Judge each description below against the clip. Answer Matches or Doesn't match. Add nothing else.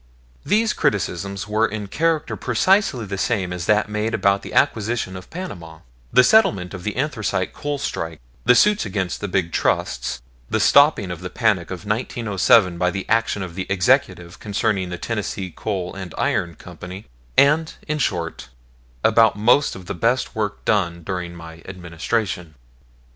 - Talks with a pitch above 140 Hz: Doesn't match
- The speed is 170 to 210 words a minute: Doesn't match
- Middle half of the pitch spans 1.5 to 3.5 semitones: Doesn't match